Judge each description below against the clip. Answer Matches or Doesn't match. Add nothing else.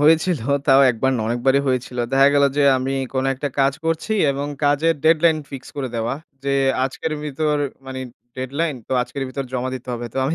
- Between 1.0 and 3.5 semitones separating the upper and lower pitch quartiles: Matches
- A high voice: Doesn't match